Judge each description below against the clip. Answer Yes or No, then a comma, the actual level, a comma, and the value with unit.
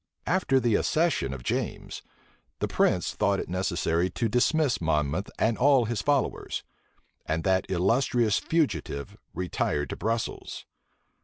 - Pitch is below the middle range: Yes, low, 105 Hz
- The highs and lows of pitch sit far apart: Yes, wide, 7.1 semitones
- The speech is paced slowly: Yes, slow, 130 wpm